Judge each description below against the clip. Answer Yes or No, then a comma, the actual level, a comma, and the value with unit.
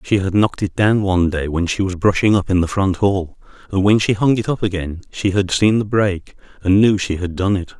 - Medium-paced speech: No, fast, 260 wpm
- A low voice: Yes, very low, 95 Hz